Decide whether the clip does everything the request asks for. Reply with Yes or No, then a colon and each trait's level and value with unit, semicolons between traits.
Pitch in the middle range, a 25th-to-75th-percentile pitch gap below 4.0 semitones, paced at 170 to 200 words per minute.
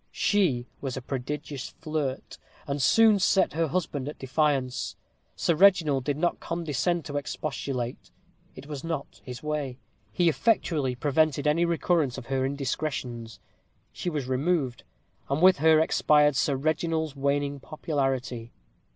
No: medium, 145 Hz; average, 3.3 semitones; slow, 135 wpm